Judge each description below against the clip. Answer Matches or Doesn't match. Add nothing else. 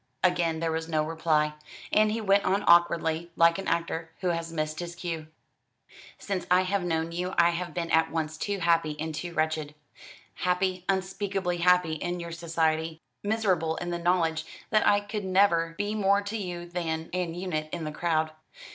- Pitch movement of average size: Doesn't match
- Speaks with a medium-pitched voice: Matches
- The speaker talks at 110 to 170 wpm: Doesn't match